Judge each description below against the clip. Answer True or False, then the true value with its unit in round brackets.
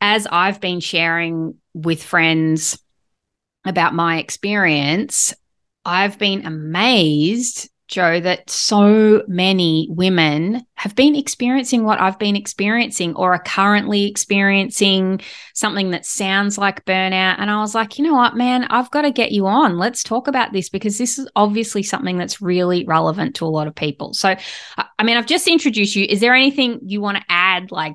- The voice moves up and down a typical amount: True (4.3 semitones)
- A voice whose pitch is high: True (195 Hz)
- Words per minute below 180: True (170 wpm)